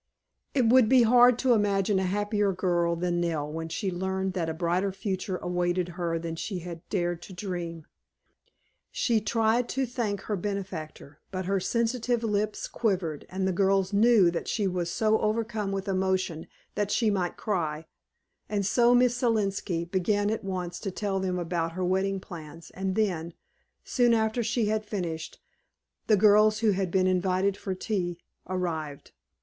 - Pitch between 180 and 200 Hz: Yes, high, 190 Hz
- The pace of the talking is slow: No, average, 165 wpm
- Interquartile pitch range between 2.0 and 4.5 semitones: Yes, average, 3.4 semitones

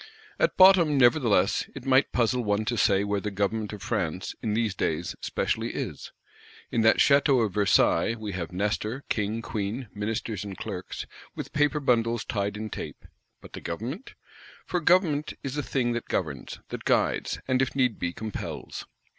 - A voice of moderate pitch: No, low, 110 Hz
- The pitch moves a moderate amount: Yes, average, 4.5 semitones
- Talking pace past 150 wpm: Yes, average, 170 wpm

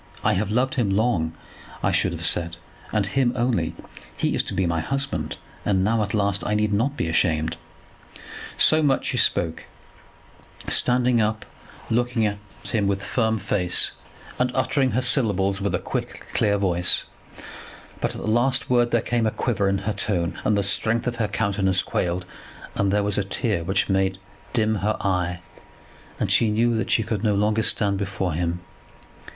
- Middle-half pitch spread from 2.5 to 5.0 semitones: Yes, average, 3.3 semitones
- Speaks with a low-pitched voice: Yes, low, 105 Hz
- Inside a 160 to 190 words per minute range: Yes, average, 180 wpm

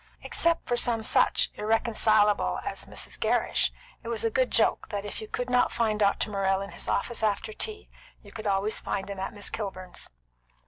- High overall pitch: Yes, high, 215 Hz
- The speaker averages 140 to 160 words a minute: No, average, 190 wpm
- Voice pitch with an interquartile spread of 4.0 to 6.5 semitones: No, narrow, 2.5 semitones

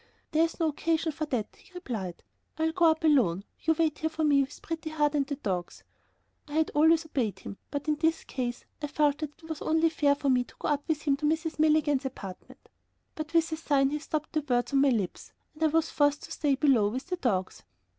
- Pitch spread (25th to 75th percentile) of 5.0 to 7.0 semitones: No, average, 2.9 semitones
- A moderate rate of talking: No, fast, 235 wpm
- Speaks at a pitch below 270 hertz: No, very high, 295 Hz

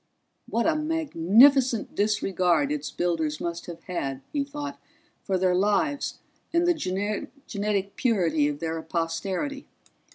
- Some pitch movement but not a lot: No, wide, 8.6 semitones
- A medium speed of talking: No, slow, 125 wpm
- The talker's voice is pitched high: Yes, high, 200 Hz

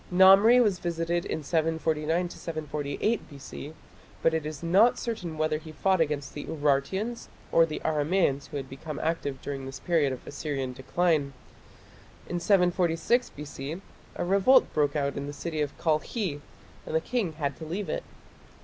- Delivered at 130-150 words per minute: No, average, 160 wpm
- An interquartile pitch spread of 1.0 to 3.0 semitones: No, average, 3.7 semitones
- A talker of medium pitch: Yes, medium, 160 Hz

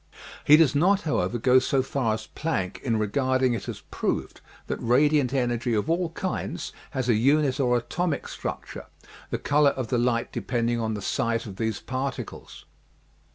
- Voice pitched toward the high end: No, low, 130 Hz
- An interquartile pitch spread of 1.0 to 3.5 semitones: No, average, 3.9 semitones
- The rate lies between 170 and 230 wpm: Yes, average, 200 wpm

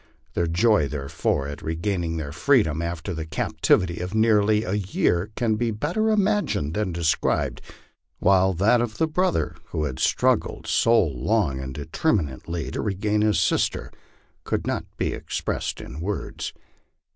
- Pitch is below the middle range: Yes, very low, 95 Hz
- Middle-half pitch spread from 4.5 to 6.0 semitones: Yes, wide, 5.5 semitones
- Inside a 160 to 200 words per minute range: No, average, 150 wpm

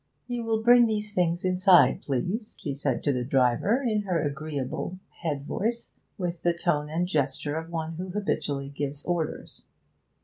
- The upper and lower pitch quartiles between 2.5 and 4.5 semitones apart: No, wide, 5.4 semitones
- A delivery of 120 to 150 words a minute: No, average, 165 wpm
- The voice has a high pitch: No, medium, 170 Hz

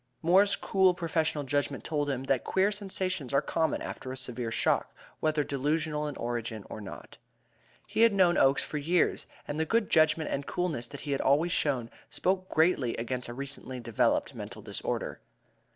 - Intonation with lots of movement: No, average, 4.8 semitones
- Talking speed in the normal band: Yes, average, 175 wpm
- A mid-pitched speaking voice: Yes, medium, 150 Hz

